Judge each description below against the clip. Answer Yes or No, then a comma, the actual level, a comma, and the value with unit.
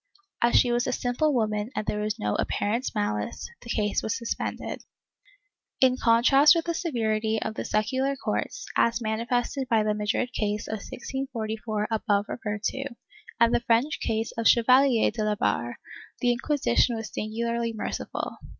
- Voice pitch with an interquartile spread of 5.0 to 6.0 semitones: No, average, 2.8 semitones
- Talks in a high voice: Yes, high, 230 Hz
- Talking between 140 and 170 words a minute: Yes, average, 165 wpm